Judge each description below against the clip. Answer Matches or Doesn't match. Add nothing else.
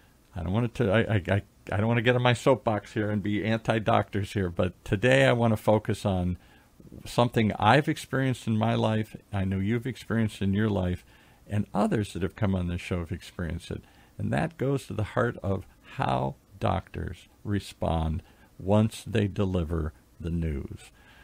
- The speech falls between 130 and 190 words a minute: Matches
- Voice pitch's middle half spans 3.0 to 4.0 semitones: Matches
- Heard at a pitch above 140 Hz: Doesn't match